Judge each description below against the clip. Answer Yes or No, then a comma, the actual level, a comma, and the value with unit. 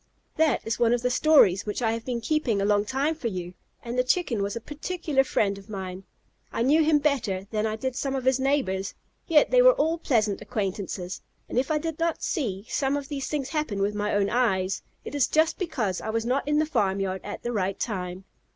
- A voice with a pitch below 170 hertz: No, high, 240 Hz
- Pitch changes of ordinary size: No, wide, 6.5 semitones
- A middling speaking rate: No, fast, 230 wpm